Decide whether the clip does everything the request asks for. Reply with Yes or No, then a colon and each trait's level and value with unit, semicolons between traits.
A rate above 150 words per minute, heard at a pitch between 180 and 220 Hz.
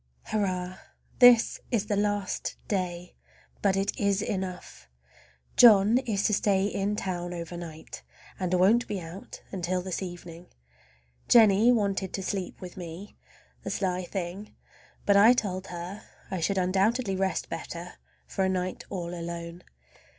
No: average, 140 wpm; high, 190 Hz